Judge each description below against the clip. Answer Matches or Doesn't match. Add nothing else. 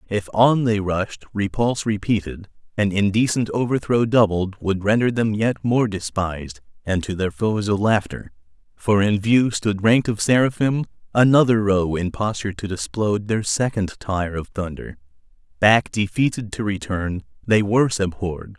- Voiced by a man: Matches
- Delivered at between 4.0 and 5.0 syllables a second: Matches